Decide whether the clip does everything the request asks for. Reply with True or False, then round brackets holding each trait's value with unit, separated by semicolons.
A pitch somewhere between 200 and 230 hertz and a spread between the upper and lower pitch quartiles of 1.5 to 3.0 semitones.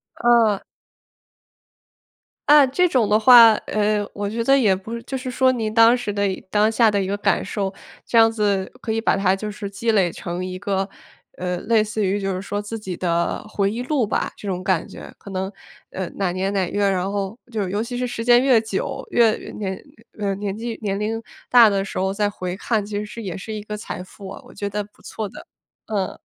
True (210 Hz; 2.7 semitones)